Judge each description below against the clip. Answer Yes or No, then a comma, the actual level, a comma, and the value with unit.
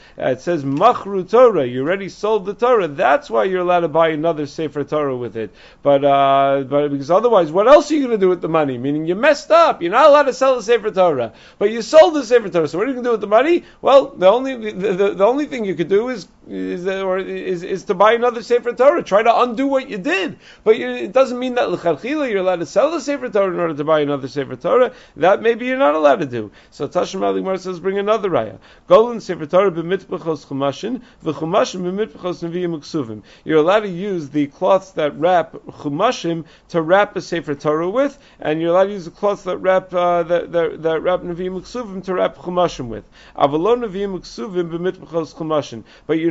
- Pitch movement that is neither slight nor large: No, wide, 5.9 semitones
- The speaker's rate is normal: No, fast, 220 wpm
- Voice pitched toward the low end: No, medium, 185 Hz